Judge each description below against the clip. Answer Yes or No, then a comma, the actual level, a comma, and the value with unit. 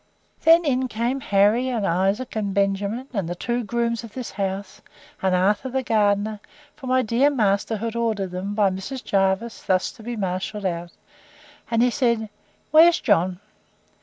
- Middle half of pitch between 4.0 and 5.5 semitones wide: No, average, 3.6 semitones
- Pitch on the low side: No, high, 215 Hz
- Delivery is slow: No, average, 165 wpm